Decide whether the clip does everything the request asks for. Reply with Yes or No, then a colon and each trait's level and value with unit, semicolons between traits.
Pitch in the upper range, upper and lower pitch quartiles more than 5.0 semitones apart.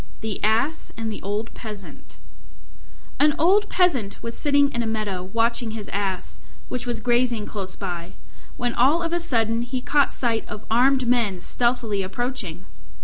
No: high, 230 Hz; average, 3.5 semitones